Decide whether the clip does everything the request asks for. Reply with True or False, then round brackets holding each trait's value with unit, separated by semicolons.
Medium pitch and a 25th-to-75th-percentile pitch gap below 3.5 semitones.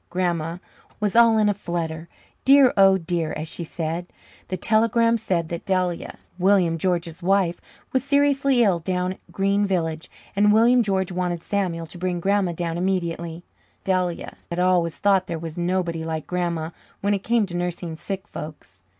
True (180 Hz; 2.9 semitones)